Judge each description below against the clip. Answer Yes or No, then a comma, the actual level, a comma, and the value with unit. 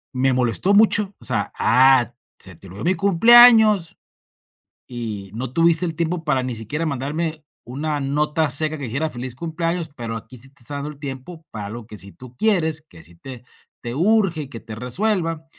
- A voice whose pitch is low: No, medium, 145 Hz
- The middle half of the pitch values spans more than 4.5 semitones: Yes, wide, 5.5 semitones